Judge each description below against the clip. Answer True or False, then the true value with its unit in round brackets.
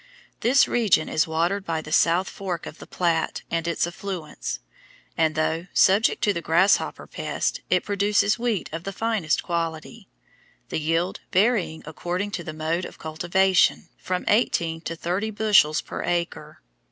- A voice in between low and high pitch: True (175 Hz)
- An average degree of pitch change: True (3.5 semitones)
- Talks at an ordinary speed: True (155 wpm)